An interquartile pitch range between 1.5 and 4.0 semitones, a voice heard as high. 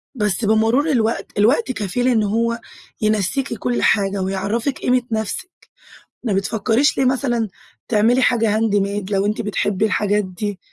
Yes: average, 2.9 semitones; high, 220 Hz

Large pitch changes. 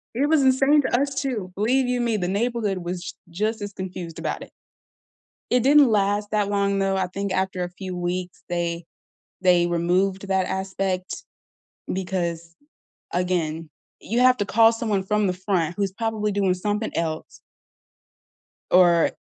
No: average, 3.3 semitones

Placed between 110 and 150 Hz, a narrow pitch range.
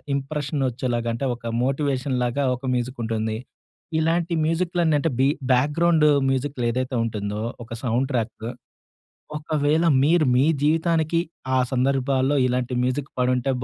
No: low, 135 Hz; average, 3.5 semitones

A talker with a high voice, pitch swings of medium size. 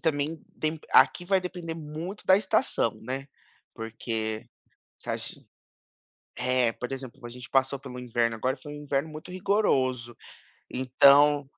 No: medium, 140 Hz; average, 4.2 semitones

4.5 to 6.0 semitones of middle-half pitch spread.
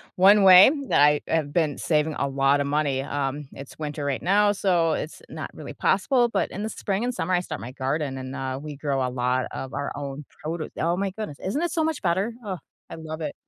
Yes: average, 5.3 semitones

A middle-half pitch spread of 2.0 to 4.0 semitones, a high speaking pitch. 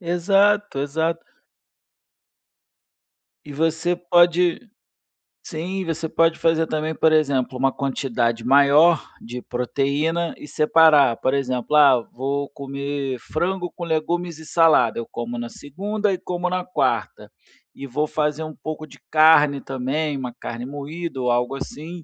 No: average, 3.6 semitones; medium, 150 Hz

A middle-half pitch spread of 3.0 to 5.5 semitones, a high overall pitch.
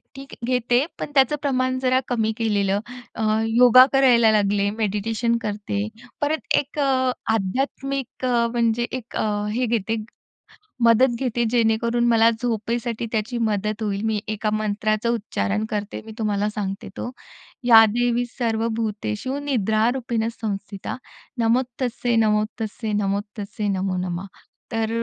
No: narrow, 2.5 semitones; high, 225 Hz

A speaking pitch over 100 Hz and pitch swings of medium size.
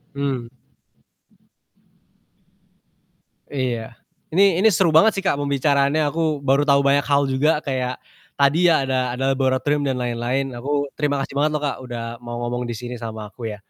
Yes: medium, 140 Hz; average, 3.0 semitones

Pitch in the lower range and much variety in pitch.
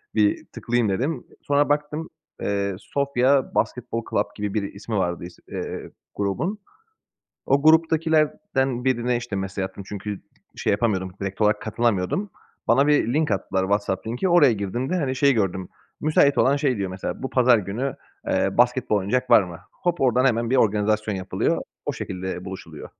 Yes: low, 120 Hz; wide, 5.8 semitones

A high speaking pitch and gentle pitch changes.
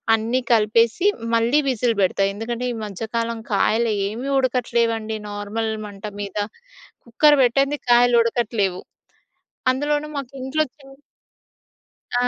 No: high, 230 Hz; average, 3.0 semitones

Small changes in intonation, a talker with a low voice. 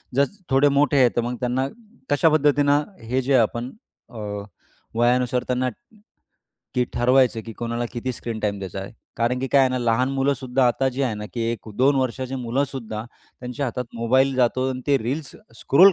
Yes: narrow, 2.2 semitones; low, 125 Hz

